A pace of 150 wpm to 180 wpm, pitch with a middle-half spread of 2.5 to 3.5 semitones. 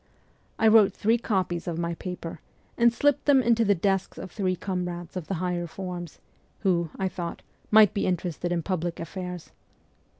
Yes: average, 170 wpm; average, 2.8 semitones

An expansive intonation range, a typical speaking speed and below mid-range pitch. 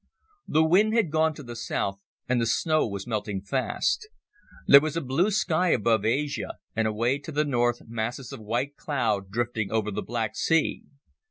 Yes: wide, 5.9 semitones; average, 180 wpm; low, 120 Hz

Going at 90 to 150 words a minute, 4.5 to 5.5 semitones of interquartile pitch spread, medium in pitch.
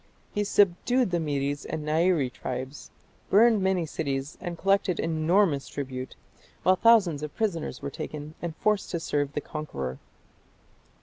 Yes: average, 145 wpm; average, 4.9 semitones; medium, 160 Hz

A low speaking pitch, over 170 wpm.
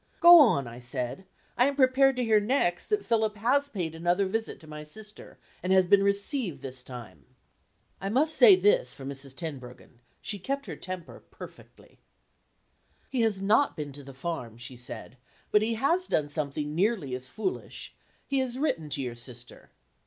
No: high, 190 Hz; average, 180 wpm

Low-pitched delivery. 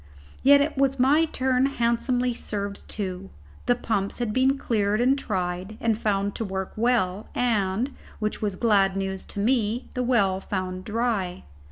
No: high, 220 Hz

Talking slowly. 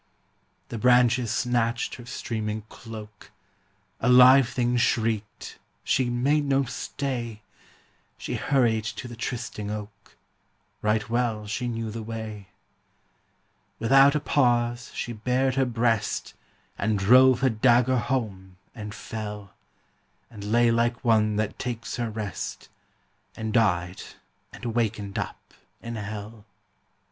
Yes: slow, 120 wpm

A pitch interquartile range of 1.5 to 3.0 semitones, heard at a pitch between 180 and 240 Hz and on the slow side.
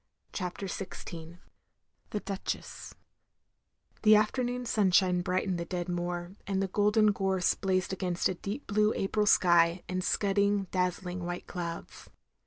Yes: narrow, 2.4 semitones; high, 190 Hz; slow, 130 wpm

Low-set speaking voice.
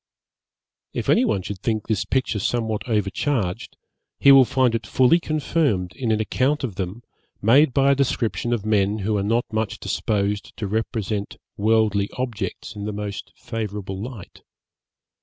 Yes: low, 110 Hz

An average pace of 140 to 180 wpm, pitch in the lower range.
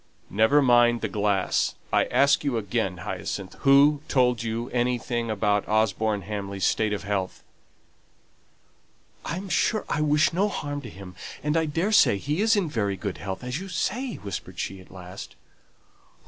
Yes: average, 160 wpm; low, 120 Hz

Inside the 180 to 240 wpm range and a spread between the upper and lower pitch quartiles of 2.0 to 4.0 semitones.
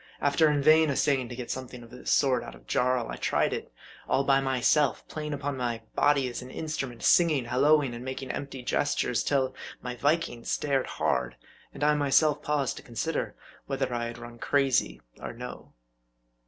Yes: average, 185 wpm; average, 2.9 semitones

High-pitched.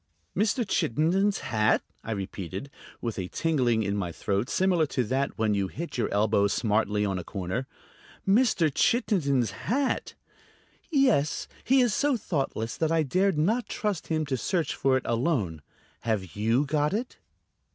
No: medium, 140 Hz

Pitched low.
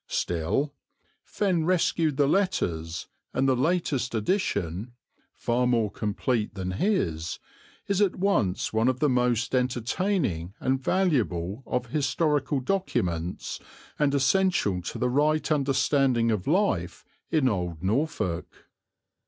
Yes: low, 130 Hz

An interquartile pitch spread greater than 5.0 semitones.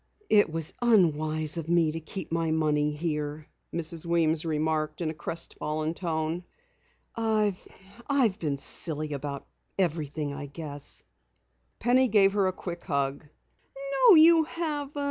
No: average, 4.1 semitones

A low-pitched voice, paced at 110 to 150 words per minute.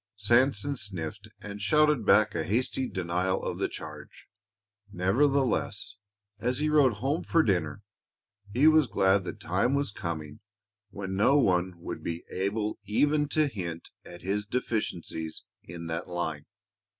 Yes: low, 100 Hz; average, 140 wpm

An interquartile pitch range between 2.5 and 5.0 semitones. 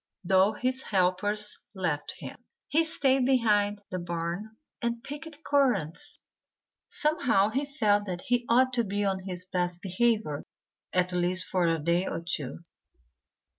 No: wide, 5.4 semitones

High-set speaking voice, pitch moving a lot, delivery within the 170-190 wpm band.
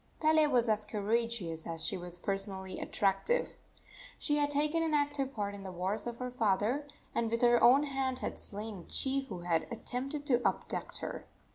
Yes: high, 235 Hz; wide, 5.9 semitones; average, 180 wpm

